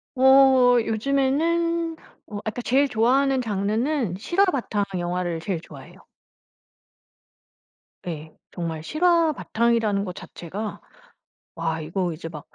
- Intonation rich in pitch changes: Yes, wide, 7.6 semitones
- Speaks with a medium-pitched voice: No, high, 225 Hz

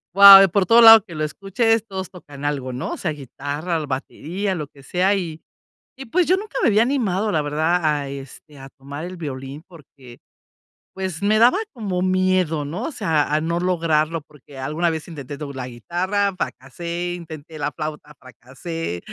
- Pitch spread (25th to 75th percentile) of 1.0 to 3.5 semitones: No, average, 4.6 semitones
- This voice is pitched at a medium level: Yes, medium, 165 Hz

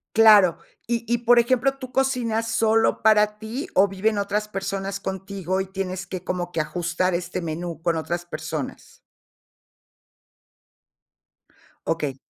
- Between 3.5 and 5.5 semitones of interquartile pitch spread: Yes, average, 4.1 semitones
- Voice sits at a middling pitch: No, high, 195 Hz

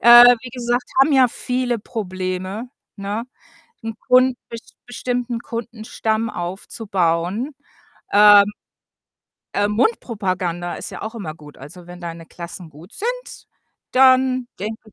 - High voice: Yes, high, 220 Hz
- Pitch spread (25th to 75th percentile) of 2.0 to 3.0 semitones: No, average, 5.0 semitones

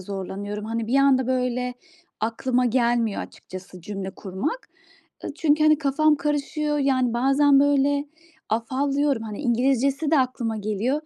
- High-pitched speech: Yes, very high, 255 Hz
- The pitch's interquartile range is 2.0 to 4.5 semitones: Yes, average, 4.2 semitones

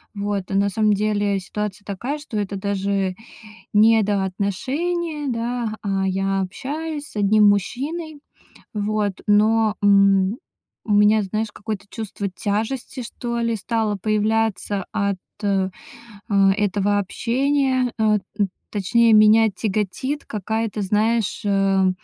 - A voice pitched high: Yes, high, 210 Hz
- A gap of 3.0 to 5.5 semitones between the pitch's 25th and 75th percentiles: No, narrow, 2.4 semitones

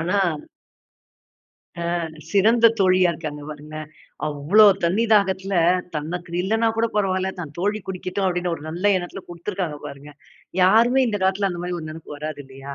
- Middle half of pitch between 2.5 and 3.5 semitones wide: No, average, 4.3 semitones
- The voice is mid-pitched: Yes, medium, 180 Hz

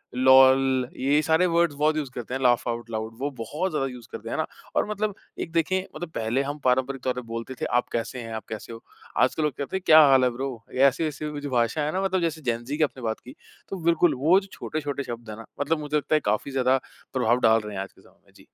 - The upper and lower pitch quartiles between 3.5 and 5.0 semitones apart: Yes, average, 4.4 semitones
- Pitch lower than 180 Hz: Yes, low, 135 Hz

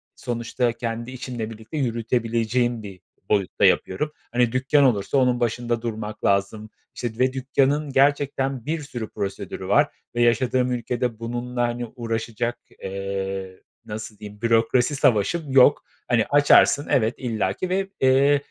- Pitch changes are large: No, average, 2.9 semitones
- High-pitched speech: No, low, 120 Hz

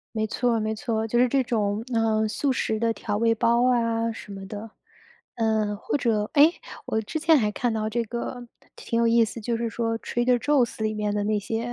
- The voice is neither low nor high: No, high, 225 Hz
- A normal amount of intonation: No, narrow, 1.8 semitones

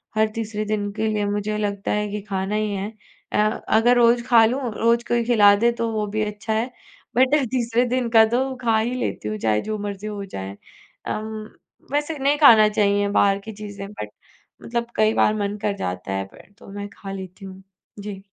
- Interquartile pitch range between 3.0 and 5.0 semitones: No, narrow, 2.5 semitones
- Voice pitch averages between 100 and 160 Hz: No, high, 215 Hz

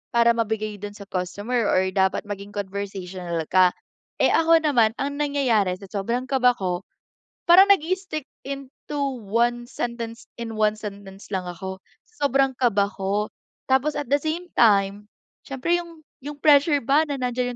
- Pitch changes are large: Yes, wide, 5.7 semitones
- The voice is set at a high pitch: Yes, high, 230 Hz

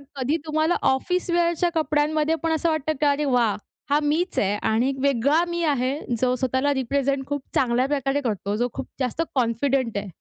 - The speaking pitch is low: No, very high, 280 Hz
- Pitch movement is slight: No, average, 3.6 semitones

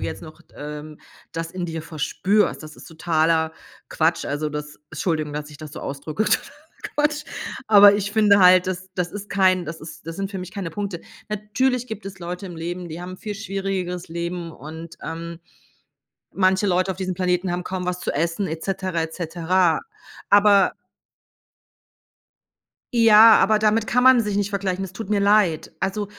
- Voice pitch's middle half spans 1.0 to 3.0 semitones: No, average, 3.6 semitones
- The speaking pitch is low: No, medium, 185 Hz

